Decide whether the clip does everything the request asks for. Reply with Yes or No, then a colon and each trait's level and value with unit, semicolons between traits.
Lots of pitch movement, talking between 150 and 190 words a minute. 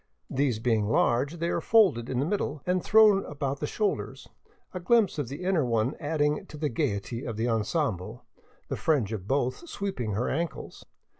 Yes: wide, 6.6 semitones; average, 180 wpm